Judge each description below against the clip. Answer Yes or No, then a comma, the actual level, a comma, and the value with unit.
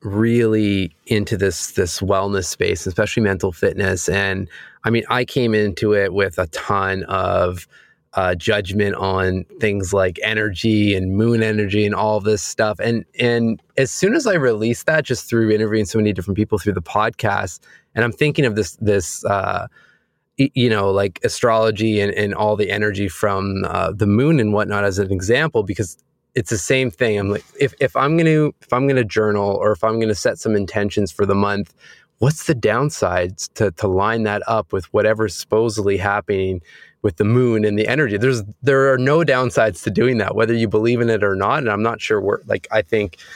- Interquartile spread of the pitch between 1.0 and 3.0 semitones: Yes, narrow, 2.4 semitones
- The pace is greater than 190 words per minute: Yes, average, 200 wpm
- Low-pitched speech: Yes, low, 105 Hz